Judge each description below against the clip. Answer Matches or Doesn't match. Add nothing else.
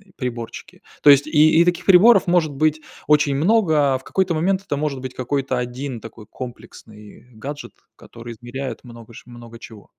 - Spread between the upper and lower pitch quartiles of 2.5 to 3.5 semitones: Doesn't match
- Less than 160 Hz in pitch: Matches